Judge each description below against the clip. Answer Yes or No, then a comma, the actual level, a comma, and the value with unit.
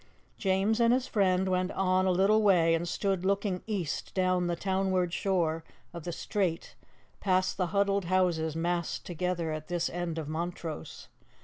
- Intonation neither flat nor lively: No, narrow, 2.2 semitones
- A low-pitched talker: No, medium, 185 Hz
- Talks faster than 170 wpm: No, average, 165 wpm